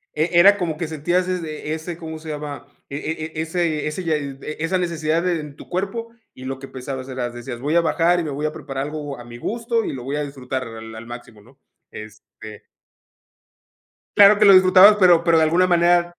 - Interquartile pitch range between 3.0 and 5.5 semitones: Yes, average, 4.5 semitones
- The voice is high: No, medium, 155 Hz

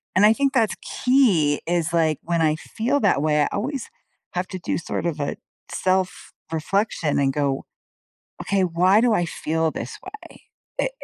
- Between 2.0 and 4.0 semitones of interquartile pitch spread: No, wide, 5.6 semitones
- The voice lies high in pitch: No, medium, 175 Hz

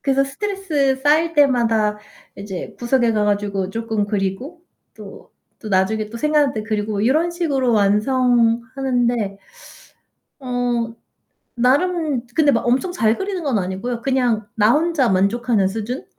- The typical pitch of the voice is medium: No, high, 240 Hz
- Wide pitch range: No, average, 4.5 semitones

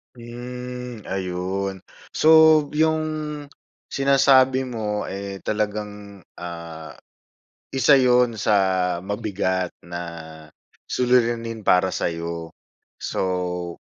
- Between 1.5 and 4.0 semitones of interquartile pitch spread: No, average, 5.2 semitones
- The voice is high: No, low, 105 Hz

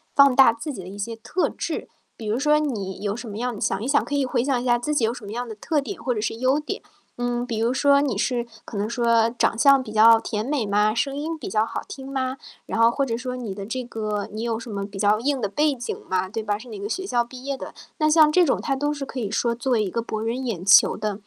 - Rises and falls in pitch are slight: No, average, 4.0 semitones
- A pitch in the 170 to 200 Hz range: No, high, 240 Hz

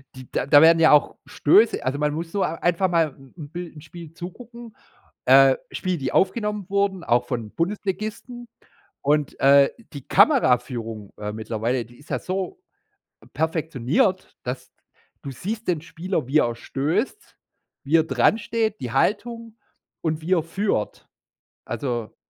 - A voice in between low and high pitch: Yes, medium, 160 Hz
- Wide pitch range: Yes, wide, 6.6 semitones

